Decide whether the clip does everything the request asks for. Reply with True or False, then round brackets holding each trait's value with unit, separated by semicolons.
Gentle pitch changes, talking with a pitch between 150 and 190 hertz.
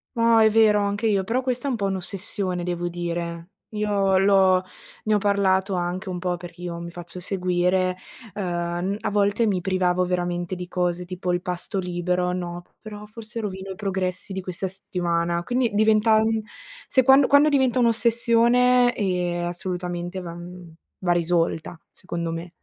False (3.2 semitones; 185 Hz)